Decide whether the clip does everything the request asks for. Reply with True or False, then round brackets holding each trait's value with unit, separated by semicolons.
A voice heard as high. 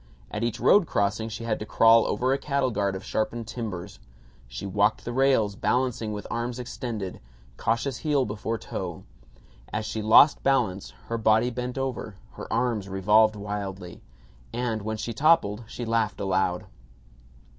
False (110 Hz)